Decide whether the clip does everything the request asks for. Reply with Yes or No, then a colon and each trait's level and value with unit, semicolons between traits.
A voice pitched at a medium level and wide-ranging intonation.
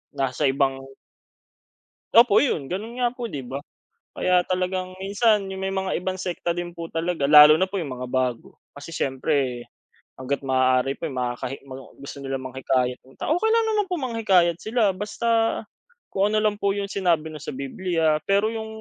Yes: medium, 175 Hz; wide, 6.7 semitones